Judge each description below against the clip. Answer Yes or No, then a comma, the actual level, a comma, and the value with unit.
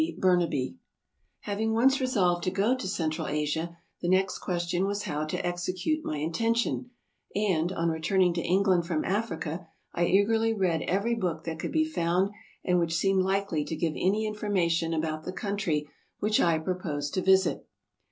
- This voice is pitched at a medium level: Yes, medium, 180 Hz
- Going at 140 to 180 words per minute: Yes, average, 170 wpm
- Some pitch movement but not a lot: Yes, average, 3.6 semitones